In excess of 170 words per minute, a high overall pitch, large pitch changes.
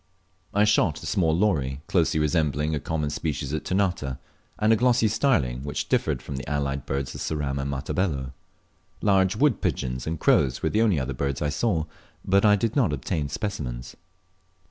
No: average, 180 wpm; very low, 75 Hz; wide, 6.4 semitones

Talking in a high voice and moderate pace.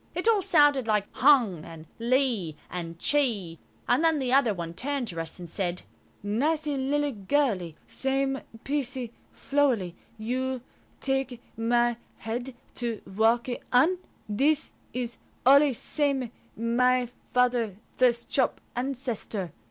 No: high, 245 Hz; slow, 120 wpm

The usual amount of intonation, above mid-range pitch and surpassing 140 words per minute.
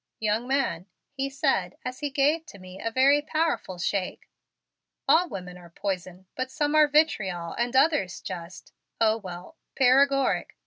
No: wide, 7.4 semitones; very high, 250 Hz; average, 150 wpm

